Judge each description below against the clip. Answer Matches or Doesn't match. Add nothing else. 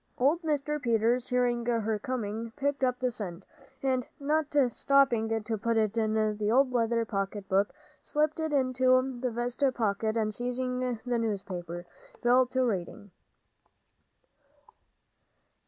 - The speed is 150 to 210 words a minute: Doesn't match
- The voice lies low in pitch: Doesn't match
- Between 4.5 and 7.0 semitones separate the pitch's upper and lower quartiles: Doesn't match